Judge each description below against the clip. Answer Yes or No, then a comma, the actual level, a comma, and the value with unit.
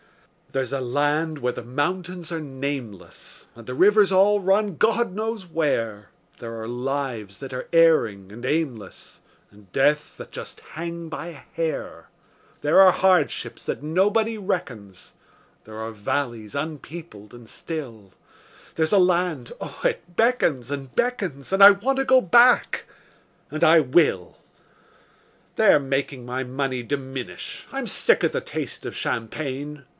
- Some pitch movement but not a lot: No, wide, 6.5 semitones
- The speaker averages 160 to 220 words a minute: No, average, 145 wpm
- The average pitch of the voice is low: No, medium, 145 Hz